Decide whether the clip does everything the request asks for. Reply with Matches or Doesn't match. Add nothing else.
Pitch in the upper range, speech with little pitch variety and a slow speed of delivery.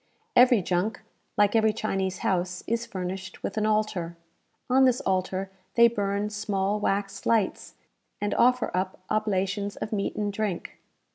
Doesn't match